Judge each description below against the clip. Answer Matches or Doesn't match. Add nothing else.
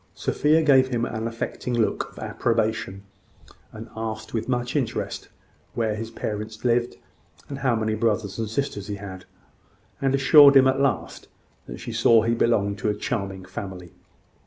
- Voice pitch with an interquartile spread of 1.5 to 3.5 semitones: Matches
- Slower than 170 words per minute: Matches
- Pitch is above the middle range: Doesn't match